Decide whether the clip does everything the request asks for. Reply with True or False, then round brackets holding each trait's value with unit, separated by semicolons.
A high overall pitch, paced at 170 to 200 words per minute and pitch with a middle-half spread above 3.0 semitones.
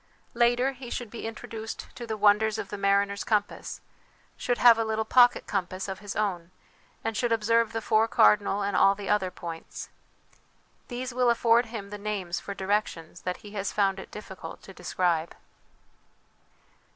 False (210 Hz; 175 wpm; 2.7 semitones)